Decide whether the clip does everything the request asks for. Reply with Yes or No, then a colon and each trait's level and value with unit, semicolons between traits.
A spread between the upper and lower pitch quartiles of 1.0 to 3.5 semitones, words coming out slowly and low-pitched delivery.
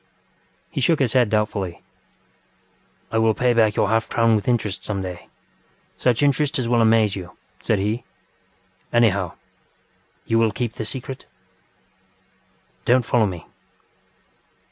Yes: average, 2.8 semitones; slow, 130 wpm; low, 115 Hz